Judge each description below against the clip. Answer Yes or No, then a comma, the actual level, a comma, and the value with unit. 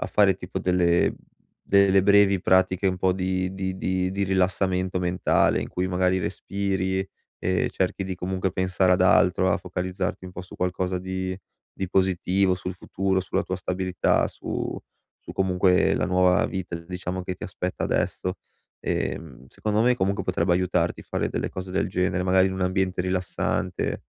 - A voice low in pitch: Yes, very low, 95 Hz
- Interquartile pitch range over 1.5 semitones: No, narrow, 0.7 semitones